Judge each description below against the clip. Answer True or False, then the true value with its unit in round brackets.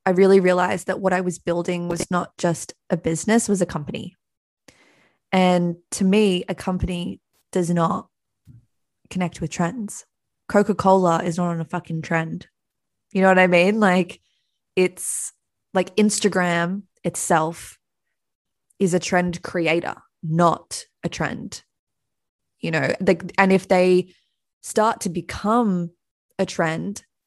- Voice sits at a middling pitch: True (180 Hz)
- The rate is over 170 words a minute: False (135 wpm)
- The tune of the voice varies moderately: False (2.0 semitones)